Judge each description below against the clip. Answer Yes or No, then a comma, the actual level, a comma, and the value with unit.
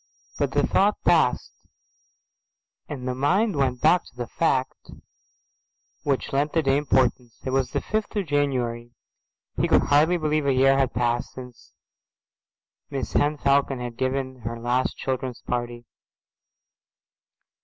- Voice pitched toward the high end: No, low, 135 Hz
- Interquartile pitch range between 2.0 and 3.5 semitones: Yes, average, 2.9 semitones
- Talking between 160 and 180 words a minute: No, average, 140 wpm